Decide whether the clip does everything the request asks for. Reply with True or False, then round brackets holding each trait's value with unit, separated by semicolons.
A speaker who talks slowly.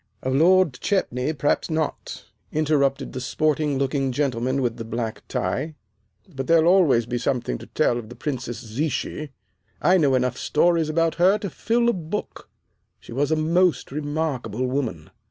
False (160 wpm)